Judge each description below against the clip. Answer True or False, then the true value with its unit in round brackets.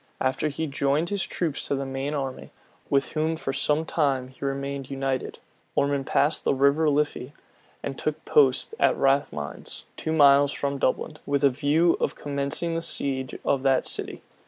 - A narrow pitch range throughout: True (1.8 semitones)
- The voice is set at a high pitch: False (140 Hz)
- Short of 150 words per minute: False (175 wpm)